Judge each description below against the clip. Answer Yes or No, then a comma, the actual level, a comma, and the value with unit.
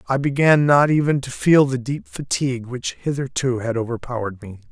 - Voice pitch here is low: Yes, low, 130 Hz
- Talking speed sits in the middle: Yes, average, 180 wpm